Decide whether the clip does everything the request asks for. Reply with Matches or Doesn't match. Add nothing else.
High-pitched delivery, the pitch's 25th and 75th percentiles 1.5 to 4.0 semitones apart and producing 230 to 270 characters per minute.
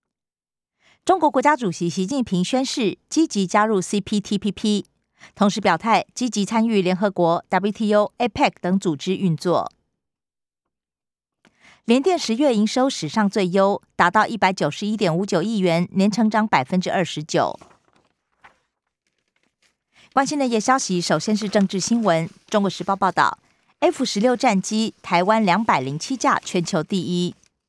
Matches